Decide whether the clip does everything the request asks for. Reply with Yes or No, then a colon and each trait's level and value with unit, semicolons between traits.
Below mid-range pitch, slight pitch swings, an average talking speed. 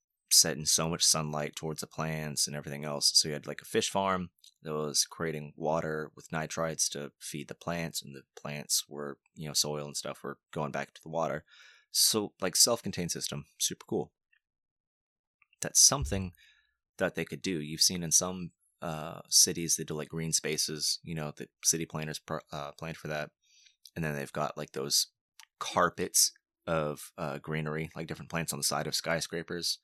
Yes: very low, 80 Hz; narrow, 1.8 semitones; average, 185 wpm